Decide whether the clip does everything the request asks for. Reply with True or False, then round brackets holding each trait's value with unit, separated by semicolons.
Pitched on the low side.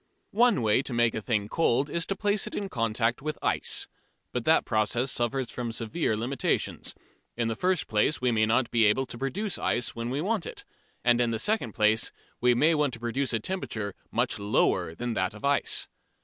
True (120 Hz)